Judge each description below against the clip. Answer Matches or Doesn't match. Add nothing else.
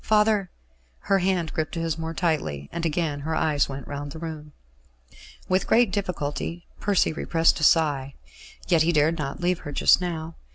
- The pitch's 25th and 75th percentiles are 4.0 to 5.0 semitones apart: Doesn't match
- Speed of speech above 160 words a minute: Matches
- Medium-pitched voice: Matches